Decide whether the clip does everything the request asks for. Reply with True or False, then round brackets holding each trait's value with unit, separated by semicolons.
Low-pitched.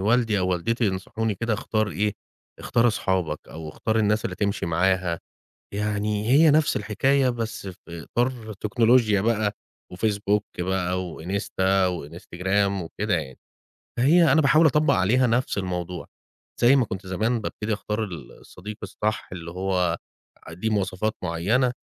True (105 Hz)